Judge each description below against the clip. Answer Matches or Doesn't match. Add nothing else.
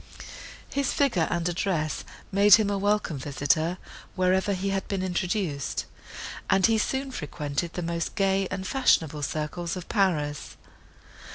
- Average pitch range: Matches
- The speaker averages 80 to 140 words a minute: Matches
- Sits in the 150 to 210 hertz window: Matches